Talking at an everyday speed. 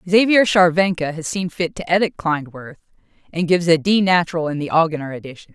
Yes: average, 185 wpm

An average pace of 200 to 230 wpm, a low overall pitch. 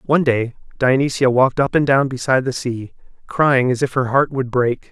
Yes: fast, 205 wpm; low, 130 Hz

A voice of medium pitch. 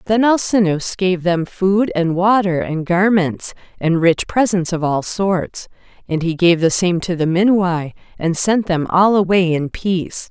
Yes: medium, 180 Hz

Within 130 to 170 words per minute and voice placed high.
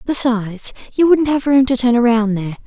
No: average, 200 wpm; high, 245 Hz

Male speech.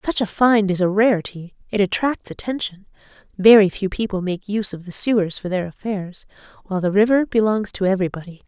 No: female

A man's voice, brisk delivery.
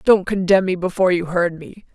No: female; fast, 215 wpm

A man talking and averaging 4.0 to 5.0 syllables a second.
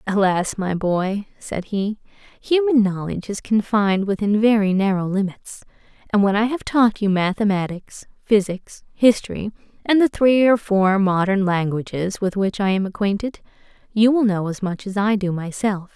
No: female; 4.7 syllables/s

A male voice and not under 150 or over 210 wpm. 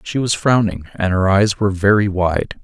Yes: male; fast, 205 wpm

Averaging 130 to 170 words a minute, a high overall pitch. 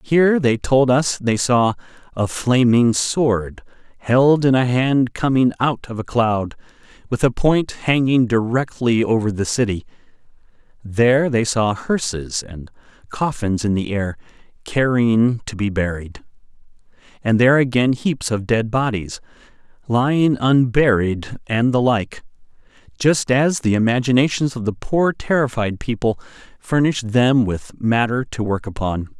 No: average, 140 wpm; low, 120 Hz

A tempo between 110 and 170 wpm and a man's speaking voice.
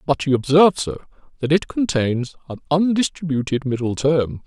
Yes: average, 150 wpm; male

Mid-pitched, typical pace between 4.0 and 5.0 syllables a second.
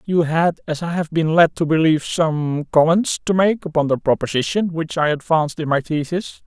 No: medium, 160 Hz; 5.2 syllables/s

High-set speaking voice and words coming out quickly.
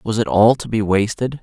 No: low, 110 Hz; fast, 255 wpm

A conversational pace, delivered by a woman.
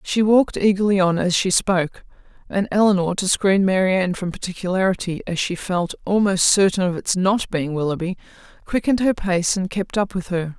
Yes: average, 180 wpm; female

